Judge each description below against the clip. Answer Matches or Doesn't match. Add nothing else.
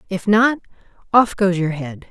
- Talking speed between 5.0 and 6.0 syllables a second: Doesn't match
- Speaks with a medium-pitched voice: Doesn't match